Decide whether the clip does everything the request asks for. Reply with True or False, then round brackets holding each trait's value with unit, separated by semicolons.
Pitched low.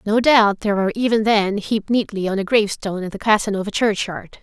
False (210 Hz)